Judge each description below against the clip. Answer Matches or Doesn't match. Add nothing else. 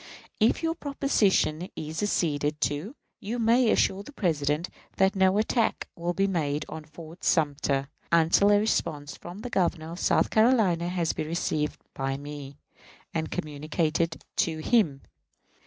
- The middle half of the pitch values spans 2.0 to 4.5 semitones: Doesn't match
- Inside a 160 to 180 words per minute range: Doesn't match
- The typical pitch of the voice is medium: Matches